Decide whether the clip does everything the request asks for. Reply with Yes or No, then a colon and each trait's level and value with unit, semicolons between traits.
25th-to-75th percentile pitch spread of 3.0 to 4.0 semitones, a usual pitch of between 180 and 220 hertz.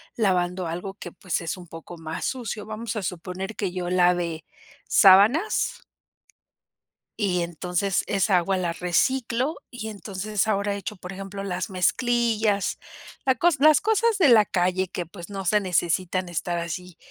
Yes: average, 3.4 semitones; high, 190 Hz